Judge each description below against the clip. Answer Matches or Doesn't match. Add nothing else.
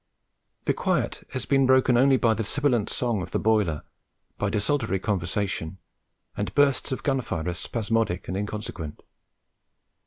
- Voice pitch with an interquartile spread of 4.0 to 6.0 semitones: Matches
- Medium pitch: Doesn't match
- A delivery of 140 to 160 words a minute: Matches